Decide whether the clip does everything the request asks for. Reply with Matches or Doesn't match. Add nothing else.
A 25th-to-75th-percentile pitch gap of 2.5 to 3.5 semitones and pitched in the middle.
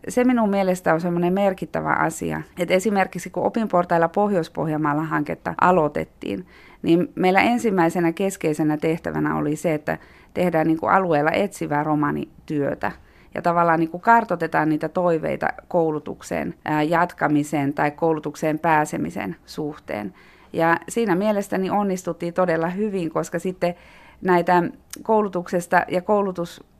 Matches